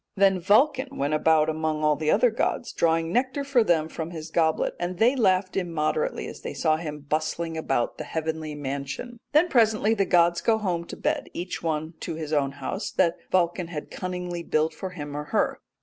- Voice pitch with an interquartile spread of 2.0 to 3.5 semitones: No, average, 3.9 semitones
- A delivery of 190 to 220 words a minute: Yes, average, 195 wpm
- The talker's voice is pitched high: No, medium, 170 Hz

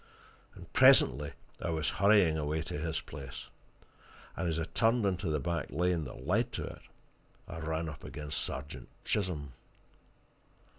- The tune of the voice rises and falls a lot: No, average, 3.3 semitones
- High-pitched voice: No, very low, 80 Hz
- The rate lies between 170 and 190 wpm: No, average, 150 wpm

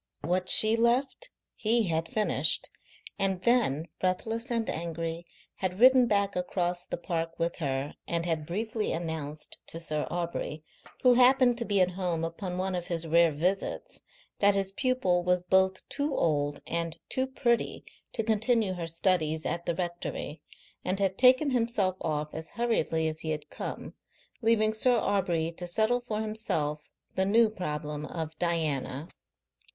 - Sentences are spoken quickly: No, average, 155 wpm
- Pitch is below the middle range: No, medium, 180 Hz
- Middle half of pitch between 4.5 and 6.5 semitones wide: Yes, average, 5.1 semitones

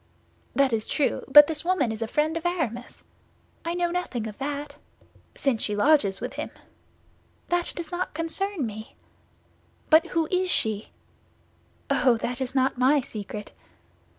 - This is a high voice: Yes, very high, 285 Hz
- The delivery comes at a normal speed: Yes, average, 150 wpm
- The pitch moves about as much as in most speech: No, wide, 6.2 semitones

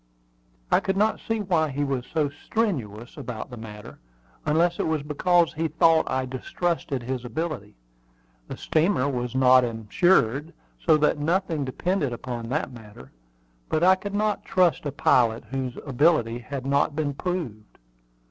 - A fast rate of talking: No, average, 155 wpm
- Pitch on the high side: No, medium, 145 Hz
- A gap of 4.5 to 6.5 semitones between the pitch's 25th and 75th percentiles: Yes, wide, 5.6 semitones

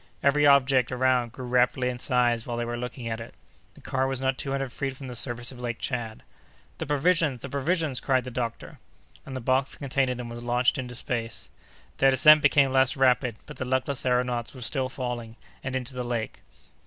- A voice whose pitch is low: Yes, low, 125 Hz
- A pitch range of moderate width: No, narrow, 1.8 semitones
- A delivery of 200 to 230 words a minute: Yes, fast, 205 wpm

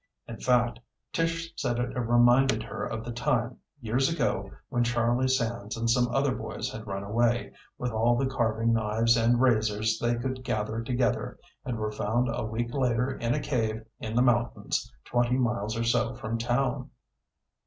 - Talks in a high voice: No, low, 120 Hz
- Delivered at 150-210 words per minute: Yes, average, 175 wpm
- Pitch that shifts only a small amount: Yes, narrow, 1.8 semitones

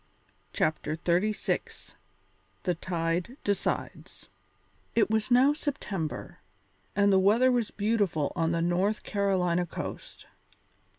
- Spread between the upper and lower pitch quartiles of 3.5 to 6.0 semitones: Yes, average, 4.1 semitones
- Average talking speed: No, slow, 105 wpm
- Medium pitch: No, high, 195 Hz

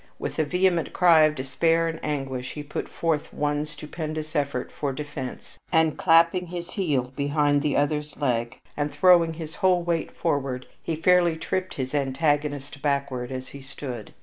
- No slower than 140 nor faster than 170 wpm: Yes, average, 165 wpm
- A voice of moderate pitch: Yes, medium, 150 Hz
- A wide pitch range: No, average, 2.9 semitones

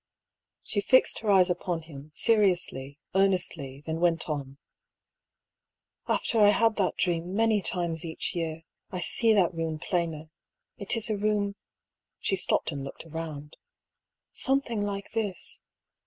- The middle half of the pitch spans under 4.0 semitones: No, average, 4.3 semitones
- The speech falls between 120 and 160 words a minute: Yes, average, 140 wpm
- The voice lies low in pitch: No, medium, 180 Hz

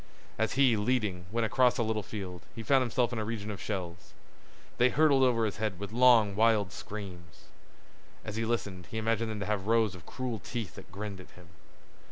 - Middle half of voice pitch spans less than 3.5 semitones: Yes, average, 2.9 semitones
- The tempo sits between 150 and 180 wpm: No, fast, 205 wpm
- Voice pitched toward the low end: Yes, low, 110 Hz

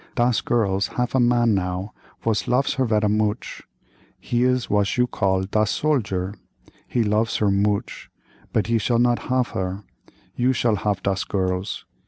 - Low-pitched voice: Yes, low, 105 Hz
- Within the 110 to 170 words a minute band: Yes, average, 160 wpm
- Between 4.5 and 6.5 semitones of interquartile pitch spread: No, average, 3.6 semitones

